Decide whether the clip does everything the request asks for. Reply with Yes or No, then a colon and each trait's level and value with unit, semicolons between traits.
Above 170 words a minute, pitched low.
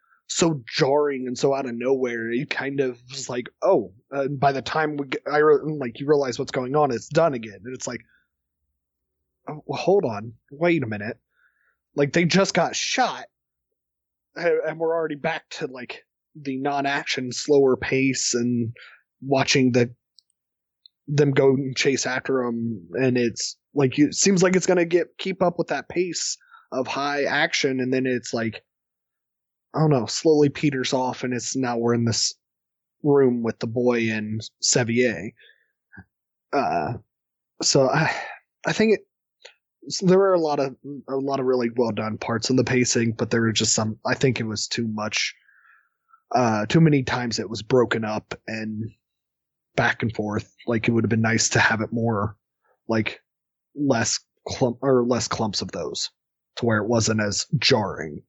Yes: average, 180 wpm; low, 130 Hz